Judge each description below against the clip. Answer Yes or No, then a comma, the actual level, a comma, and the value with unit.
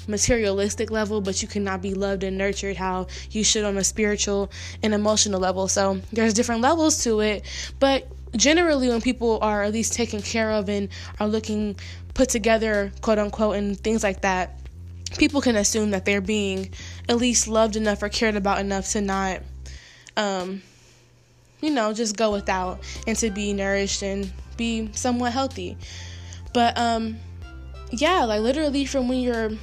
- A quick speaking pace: No, average, 170 wpm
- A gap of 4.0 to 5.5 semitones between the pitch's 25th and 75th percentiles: No, average, 2.9 semitones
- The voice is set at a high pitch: Yes, high, 210 Hz